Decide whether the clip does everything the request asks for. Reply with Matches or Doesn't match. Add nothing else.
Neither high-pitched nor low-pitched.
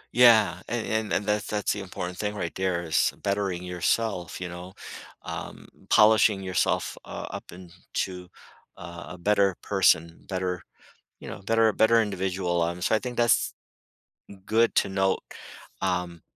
Doesn't match